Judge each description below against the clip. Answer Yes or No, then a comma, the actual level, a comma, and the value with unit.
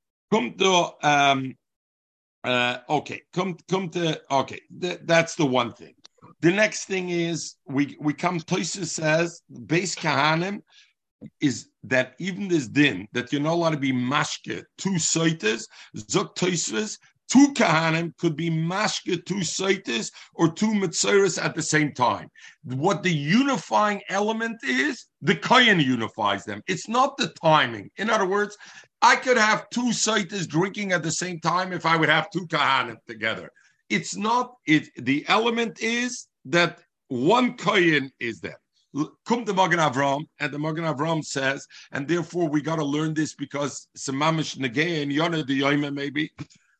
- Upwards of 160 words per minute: No, average, 145 wpm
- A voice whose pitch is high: No, medium, 165 Hz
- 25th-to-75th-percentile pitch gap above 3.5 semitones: Yes, average, 4.8 semitones